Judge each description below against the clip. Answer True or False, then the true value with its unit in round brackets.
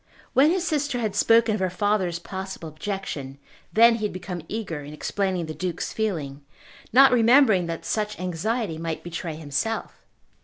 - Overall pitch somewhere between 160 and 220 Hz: True (190 Hz)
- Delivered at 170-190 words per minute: False (160 wpm)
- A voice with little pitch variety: False (5.2 semitones)